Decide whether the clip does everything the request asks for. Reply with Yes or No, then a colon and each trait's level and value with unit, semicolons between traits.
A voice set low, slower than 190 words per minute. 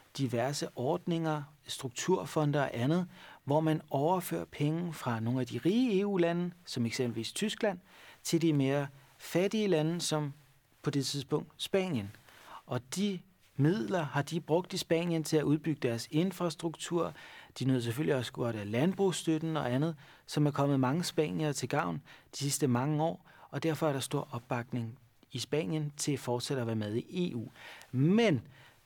No: medium, 150 Hz; average, 160 wpm